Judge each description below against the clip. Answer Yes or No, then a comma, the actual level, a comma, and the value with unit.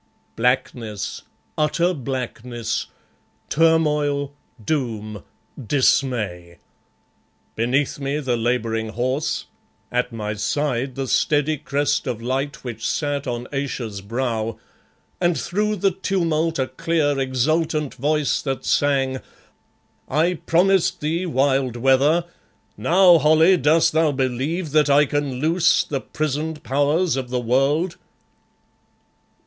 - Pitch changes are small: No, average, 4.0 semitones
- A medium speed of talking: No, slow, 110 wpm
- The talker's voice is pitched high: No, medium, 140 Hz